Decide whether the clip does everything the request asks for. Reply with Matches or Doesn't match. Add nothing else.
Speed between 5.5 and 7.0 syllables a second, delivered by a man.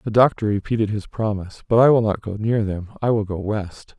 Matches